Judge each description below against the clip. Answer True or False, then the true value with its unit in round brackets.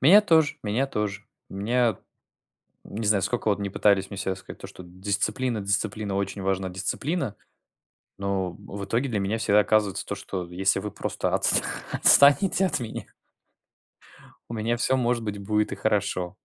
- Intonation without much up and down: False (3.3 semitones)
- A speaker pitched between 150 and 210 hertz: False (105 Hz)